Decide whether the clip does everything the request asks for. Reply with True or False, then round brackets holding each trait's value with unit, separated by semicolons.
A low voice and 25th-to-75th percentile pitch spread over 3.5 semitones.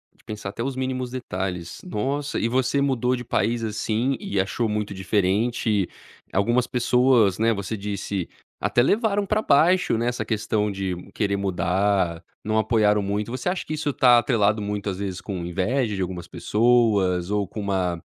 True (105 Hz; 3.9 semitones)